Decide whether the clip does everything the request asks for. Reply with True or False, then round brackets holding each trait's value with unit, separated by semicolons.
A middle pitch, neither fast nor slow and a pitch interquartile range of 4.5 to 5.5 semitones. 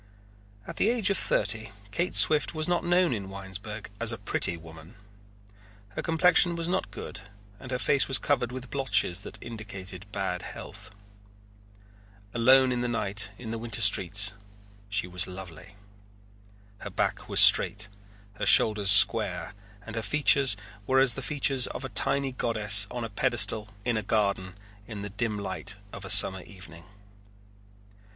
False (110 Hz; 160 wpm; 5.0 semitones)